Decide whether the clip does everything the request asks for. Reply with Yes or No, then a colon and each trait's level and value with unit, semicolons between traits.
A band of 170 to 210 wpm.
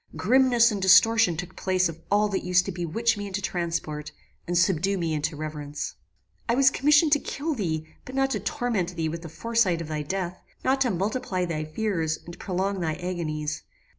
Yes: average, 195 wpm